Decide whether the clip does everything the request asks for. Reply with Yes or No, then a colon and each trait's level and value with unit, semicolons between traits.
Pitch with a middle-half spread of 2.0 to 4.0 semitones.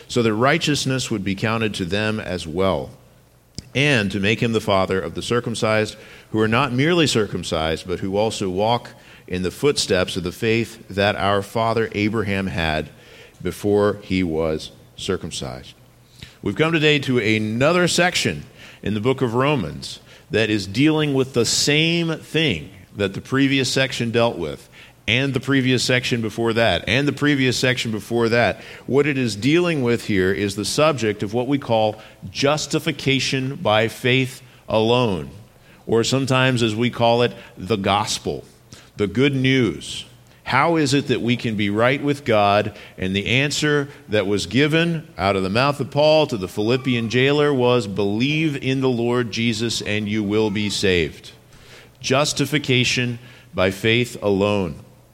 No: average, 4.5 semitones